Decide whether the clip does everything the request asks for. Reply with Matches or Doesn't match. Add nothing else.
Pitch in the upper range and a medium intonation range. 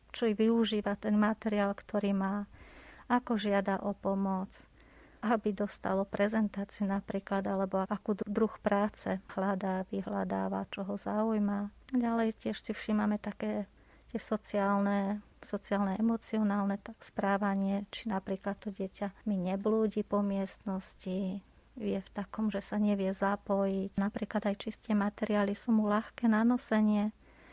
Doesn't match